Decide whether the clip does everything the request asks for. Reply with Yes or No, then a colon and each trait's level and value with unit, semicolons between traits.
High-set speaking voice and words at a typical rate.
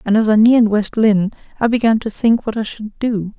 No: high, 220 Hz; fast, 250 wpm